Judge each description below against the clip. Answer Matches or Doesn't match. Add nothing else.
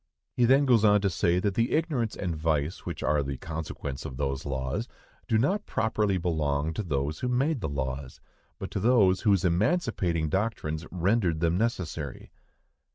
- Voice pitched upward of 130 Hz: Doesn't match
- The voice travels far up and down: Matches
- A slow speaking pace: Doesn't match